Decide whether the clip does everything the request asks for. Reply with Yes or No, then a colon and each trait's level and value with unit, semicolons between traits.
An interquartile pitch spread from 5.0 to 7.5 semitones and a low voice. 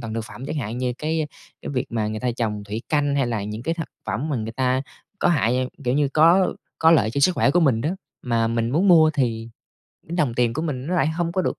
Yes: wide, 5.4 semitones; low, 130 Hz